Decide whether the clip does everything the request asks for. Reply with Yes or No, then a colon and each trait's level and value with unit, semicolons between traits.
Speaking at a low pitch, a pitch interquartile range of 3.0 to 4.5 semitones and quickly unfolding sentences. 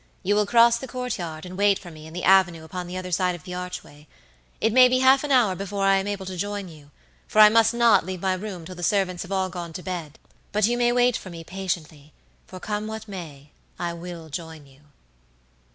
No: medium, 185 Hz; average, 3.5 semitones; fast, 235 wpm